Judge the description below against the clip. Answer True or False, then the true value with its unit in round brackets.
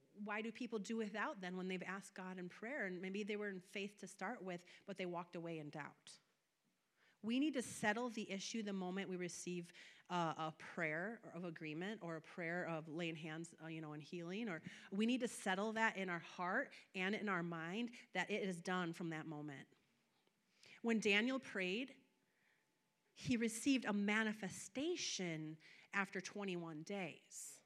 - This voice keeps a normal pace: True (180 wpm)